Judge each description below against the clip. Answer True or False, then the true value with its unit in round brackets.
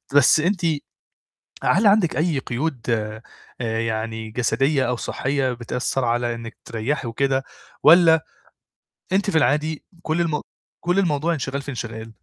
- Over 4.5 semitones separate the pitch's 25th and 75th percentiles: True (5.3 semitones)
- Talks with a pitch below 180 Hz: True (135 Hz)